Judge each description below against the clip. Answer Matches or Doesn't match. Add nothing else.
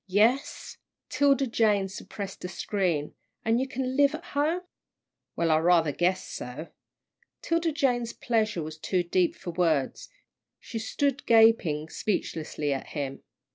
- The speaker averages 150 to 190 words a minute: Doesn't match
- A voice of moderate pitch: Doesn't match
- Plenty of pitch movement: Matches